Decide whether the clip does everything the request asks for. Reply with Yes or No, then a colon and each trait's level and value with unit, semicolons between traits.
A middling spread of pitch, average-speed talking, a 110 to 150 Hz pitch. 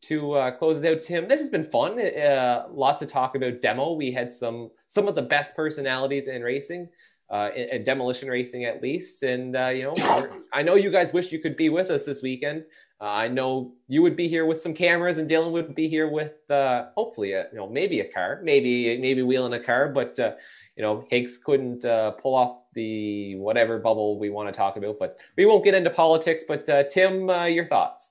No: average, 5.0 semitones; fast, 230 wpm; medium, 140 Hz